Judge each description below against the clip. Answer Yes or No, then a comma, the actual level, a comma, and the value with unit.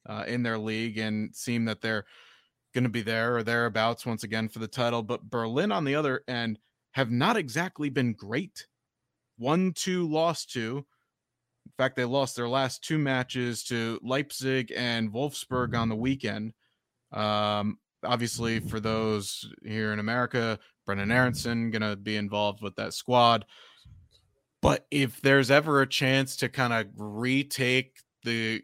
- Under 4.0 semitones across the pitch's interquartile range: Yes, average, 3.1 semitones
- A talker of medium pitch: No, low, 120 Hz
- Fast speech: No, average, 160 wpm